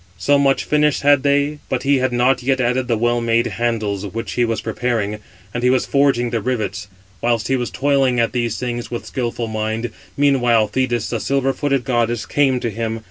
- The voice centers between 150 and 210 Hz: No, low, 120 Hz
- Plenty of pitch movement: No, narrow, 2.5 semitones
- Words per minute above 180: Yes, average, 200 wpm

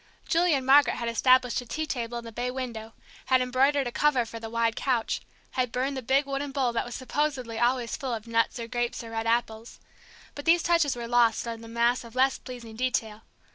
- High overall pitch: Yes, high, 245 Hz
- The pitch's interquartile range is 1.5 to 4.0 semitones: Yes, narrow, 2.5 semitones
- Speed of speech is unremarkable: No, fast, 220 wpm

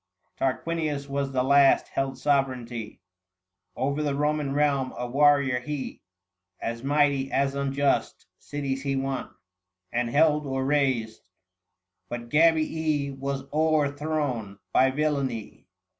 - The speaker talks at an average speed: No, slow, 115 wpm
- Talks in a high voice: No, medium, 140 Hz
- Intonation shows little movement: Yes, narrow, 1.9 semitones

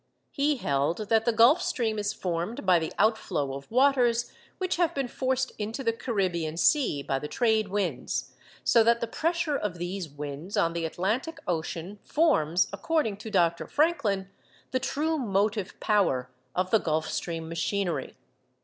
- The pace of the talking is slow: No, average, 160 wpm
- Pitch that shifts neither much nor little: No, wide, 6.7 semitones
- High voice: Yes, high, 205 Hz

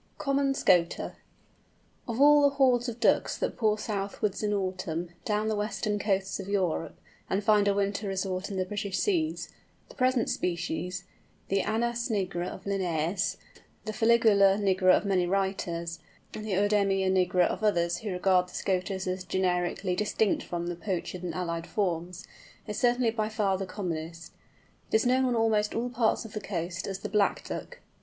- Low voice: No, high, 195 Hz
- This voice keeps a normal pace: Yes, average, 170 wpm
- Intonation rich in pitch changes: No, average, 3.1 semitones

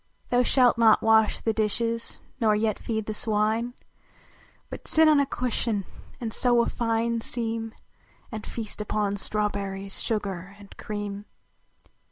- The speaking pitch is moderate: No, high, 220 Hz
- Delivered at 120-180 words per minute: Yes, average, 140 wpm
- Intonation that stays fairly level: Yes, narrow, 2.0 semitones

